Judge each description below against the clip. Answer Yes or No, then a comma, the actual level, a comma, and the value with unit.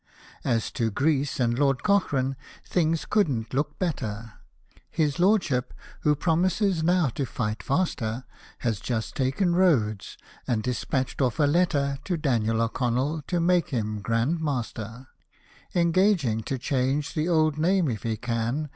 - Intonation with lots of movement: Yes, wide, 5.9 semitones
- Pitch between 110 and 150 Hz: Yes, low, 135 Hz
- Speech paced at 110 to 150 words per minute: Yes, average, 145 wpm